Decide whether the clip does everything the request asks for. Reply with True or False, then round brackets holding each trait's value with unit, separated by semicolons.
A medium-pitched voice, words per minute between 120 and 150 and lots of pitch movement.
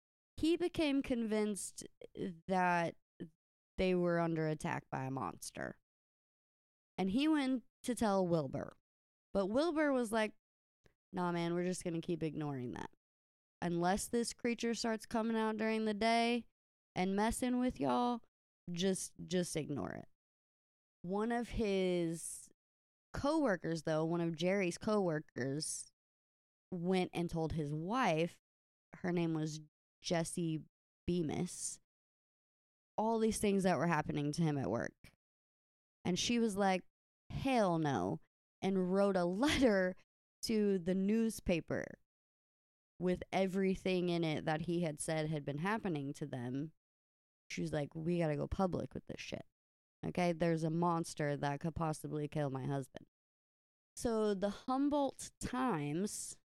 True (175 Hz; 135 wpm; 5.7 semitones)